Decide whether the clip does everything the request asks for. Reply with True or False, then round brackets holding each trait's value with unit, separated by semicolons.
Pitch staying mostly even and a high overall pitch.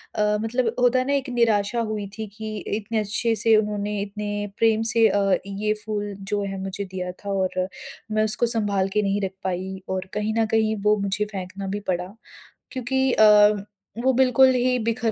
True (2.3 semitones; 210 Hz)